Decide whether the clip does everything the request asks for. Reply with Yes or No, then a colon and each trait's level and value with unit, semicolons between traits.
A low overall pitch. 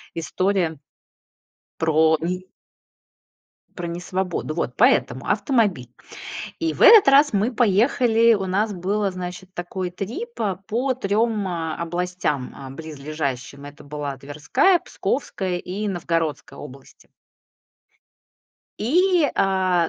No: medium, 185 Hz